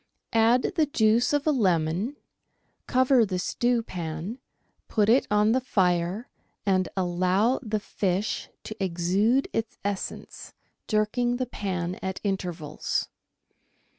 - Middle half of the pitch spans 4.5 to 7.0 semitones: Yes, average, 4.9 semitones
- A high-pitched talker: Yes, high, 210 Hz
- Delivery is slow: Yes, slow, 115 wpm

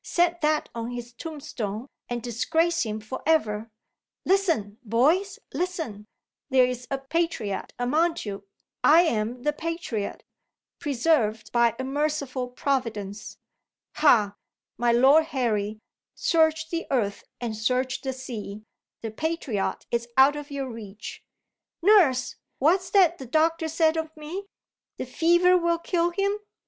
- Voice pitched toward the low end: No, very high, 270 Hz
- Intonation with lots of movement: Yes, wide, 6.0 semitones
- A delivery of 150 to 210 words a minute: No, slow, 135 wpm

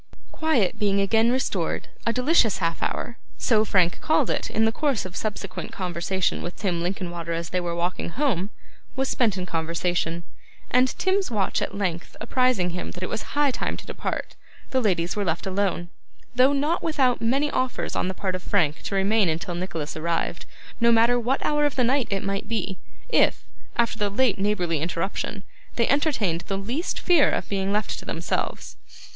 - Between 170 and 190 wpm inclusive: Yes, average, 185 wpm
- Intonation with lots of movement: Yes, wide, 5.9 semitones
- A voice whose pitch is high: Yes, high, 200 Hz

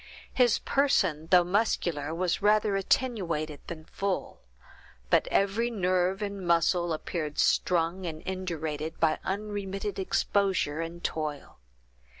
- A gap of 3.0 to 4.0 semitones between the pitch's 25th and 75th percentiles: Yes, average, 3.6 semitones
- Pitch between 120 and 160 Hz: No, medium, 180 Hz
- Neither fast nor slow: No, slow, 115 wpm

